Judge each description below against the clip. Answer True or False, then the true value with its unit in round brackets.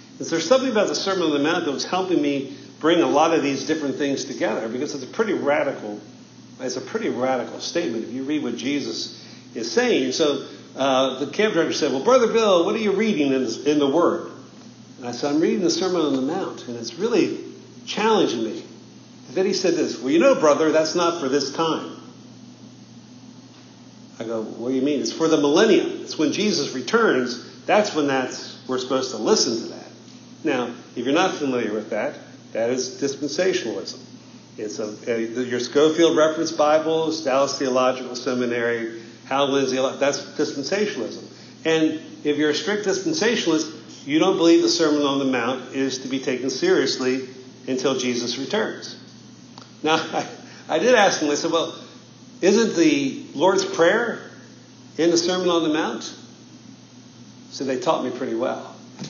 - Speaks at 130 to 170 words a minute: False (180 wpm)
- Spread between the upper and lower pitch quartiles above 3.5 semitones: True (4.4 semitones)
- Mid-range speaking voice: True (145 Hz)